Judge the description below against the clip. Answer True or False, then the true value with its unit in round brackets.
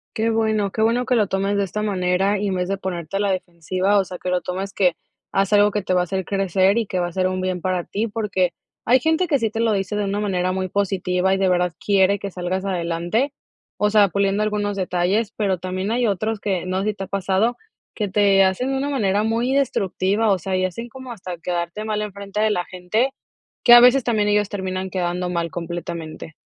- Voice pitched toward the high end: True (195 Hz)